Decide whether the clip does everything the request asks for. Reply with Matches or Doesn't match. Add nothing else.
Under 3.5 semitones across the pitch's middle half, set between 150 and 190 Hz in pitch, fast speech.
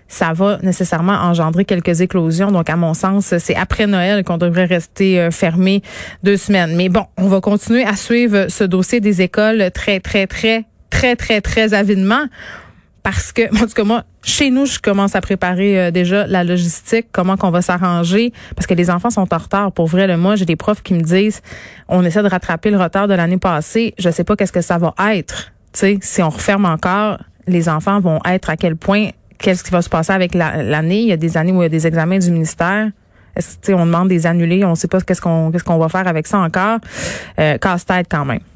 Matches